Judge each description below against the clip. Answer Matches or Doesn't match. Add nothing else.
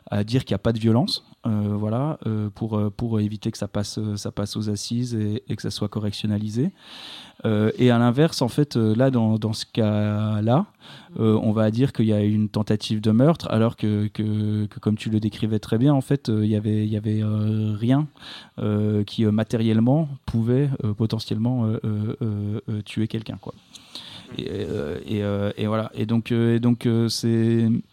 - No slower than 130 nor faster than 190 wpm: Doesn't match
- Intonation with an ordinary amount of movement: Doesn't match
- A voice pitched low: Matches